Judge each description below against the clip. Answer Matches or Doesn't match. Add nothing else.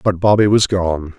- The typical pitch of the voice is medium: Doesn't match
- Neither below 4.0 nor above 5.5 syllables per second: Matches